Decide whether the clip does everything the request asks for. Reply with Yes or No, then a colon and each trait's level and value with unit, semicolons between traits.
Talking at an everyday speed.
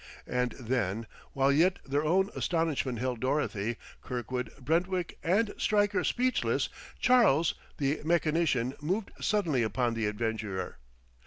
No: slow, 115 wpm